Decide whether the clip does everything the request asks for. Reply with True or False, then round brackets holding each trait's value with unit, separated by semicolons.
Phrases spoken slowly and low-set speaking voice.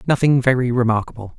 True (130 wpm; 125 Hz)